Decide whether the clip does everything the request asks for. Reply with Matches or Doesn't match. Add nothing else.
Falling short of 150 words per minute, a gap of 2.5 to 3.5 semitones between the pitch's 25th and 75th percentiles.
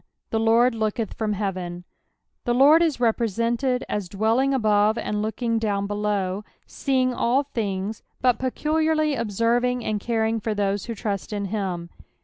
Matches